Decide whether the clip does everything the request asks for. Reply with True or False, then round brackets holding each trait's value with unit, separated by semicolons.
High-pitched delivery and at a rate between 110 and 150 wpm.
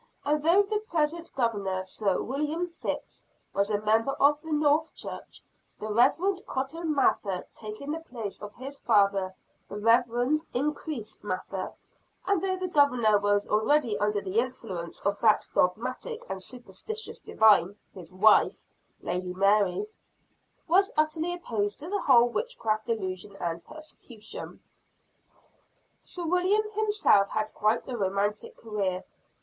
True (235 Hz; 135 wpm)